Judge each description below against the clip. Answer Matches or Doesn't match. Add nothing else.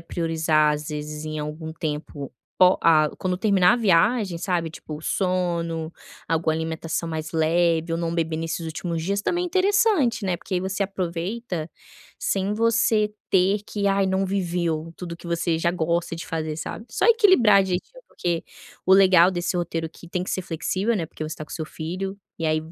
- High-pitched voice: Doesn't match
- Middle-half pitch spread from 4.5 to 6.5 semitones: Doesn't match